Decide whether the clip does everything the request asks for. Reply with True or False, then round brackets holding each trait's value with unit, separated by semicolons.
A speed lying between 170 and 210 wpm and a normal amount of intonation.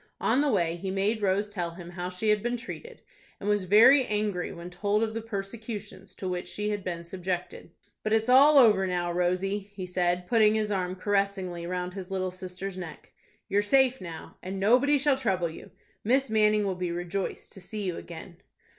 True (200 wpm; 3.1 semitones)